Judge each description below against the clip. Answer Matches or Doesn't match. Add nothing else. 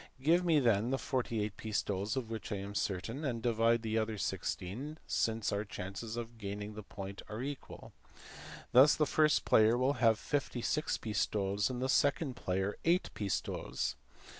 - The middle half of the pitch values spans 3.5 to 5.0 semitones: Matches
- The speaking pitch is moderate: Doesn't match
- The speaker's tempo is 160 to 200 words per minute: Matches